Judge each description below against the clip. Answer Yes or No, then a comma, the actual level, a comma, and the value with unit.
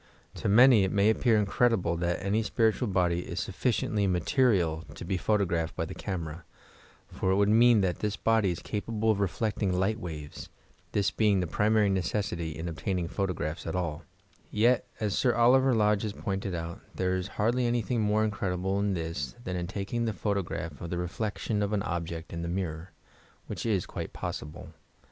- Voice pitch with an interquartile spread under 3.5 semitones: No, average, 3.8 semitones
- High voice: No, low, 100 Hz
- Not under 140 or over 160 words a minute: No, average, 185 wpm